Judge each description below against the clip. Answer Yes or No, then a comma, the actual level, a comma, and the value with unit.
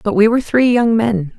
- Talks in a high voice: Yes, high, 215 Hz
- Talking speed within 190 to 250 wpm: No, fast, 260 wpm